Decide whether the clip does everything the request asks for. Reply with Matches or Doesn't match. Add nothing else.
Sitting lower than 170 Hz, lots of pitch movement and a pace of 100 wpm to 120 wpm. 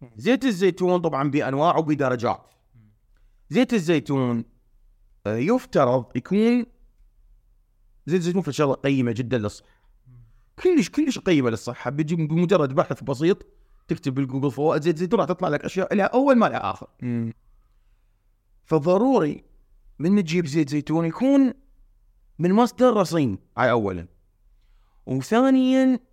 Matches